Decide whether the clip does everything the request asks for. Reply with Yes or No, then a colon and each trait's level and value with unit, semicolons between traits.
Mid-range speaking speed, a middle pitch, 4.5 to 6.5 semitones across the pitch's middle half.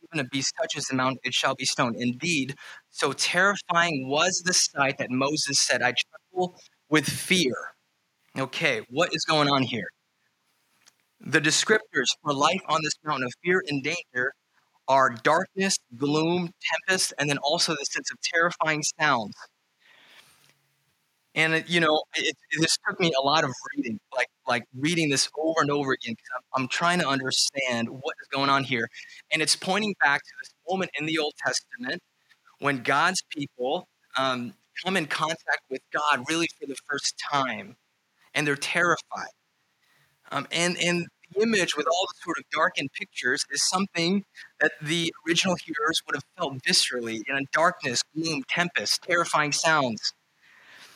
No: average, 165 wpm; medium, 155 Hz; average, 4.1 semitones